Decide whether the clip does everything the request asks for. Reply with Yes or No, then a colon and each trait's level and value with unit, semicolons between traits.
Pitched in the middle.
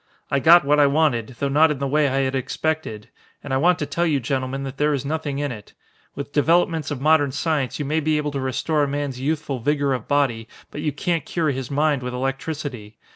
Yes: medium, 145 Hz